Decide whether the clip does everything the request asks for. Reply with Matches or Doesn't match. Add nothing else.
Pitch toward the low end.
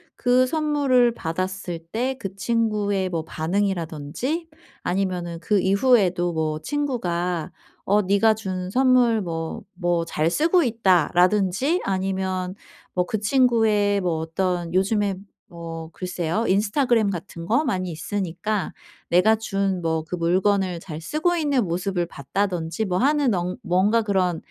Doesn't match